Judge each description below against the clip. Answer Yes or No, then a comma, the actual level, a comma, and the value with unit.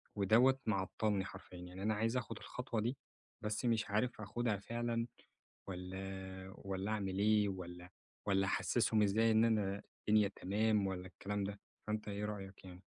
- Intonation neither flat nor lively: No, narrow, 2.3 semitones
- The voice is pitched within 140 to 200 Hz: No, low, 105 Hz